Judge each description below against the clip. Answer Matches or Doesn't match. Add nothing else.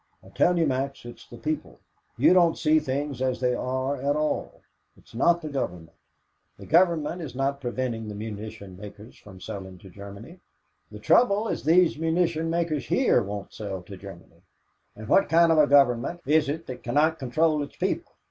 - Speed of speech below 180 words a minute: Doesn't match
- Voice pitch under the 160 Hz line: Matches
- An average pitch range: Doesn't match